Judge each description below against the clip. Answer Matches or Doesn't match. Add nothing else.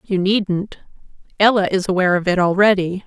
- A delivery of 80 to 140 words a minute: Matches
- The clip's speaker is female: Matches